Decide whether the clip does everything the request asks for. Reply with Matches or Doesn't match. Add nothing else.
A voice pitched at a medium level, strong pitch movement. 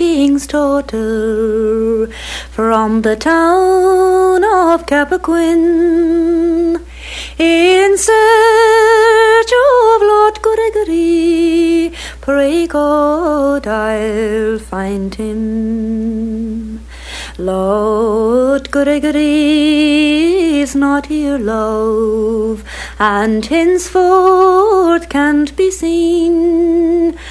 Doesn't match